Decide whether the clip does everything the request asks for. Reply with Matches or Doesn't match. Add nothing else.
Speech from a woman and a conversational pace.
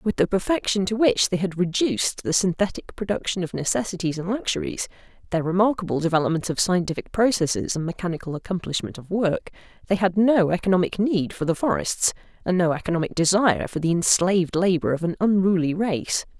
Matches